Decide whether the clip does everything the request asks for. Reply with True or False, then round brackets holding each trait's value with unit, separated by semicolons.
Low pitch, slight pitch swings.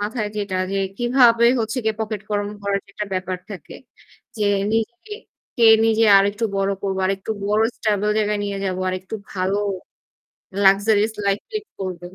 False (205 Hz; 2.2 semitones)